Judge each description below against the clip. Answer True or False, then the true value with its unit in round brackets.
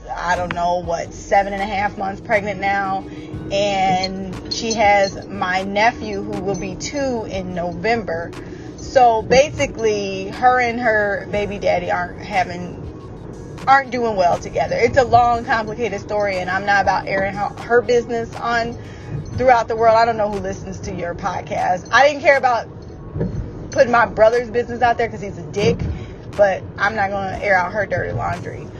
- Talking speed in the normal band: True (175 wpm)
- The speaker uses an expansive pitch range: False (3.6 semitones)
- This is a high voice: True (205 Hz)